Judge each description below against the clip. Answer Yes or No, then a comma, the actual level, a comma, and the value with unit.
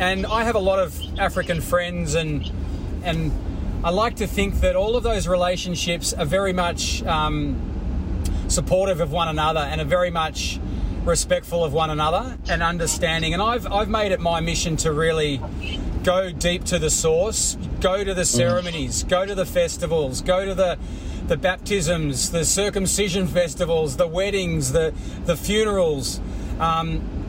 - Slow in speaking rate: No, average, 160 wpm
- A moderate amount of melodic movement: Yes, average, 3.6 semitones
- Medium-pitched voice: Yes, medium, 170 Hz